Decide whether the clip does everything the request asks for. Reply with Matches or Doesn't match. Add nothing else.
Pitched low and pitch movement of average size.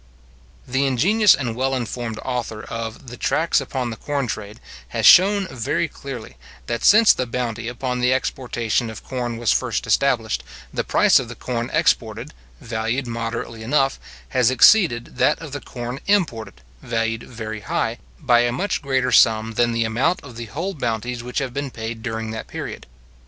Matches